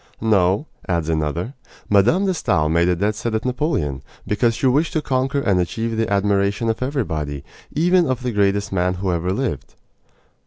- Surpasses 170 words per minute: Yes, average, 180 wpm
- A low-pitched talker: Yes, low, 105 Hz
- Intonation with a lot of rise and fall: Yes, wide, 6.2 semitones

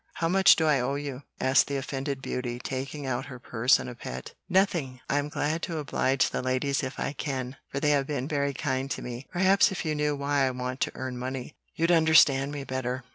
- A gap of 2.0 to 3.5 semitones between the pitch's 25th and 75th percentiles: Yes, narrow, 2.4 semitones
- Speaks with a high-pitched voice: No, low, 135 Hz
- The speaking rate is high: Yes, fast, 225 wpm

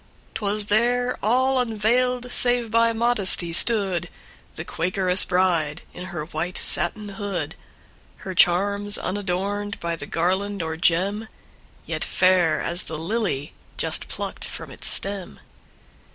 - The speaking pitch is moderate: No, high, 200 Hz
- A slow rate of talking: Yes, slow, 120 wpm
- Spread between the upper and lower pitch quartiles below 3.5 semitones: No, average, 3.8 semitones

